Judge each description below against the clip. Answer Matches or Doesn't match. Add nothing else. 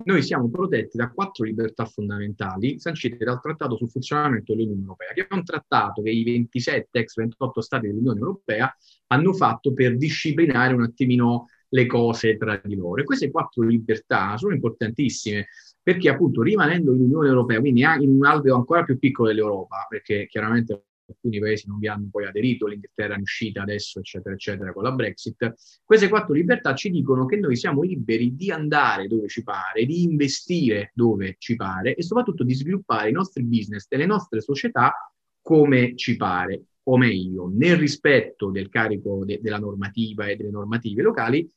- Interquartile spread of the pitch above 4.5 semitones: Matches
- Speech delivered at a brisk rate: Matches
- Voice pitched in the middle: Doesn't match